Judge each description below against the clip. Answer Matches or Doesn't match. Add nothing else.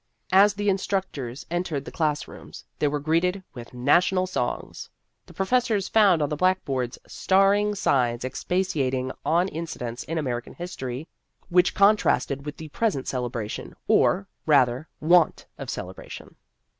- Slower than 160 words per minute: Matches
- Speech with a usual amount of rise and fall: Doesn't match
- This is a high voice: Doesn't match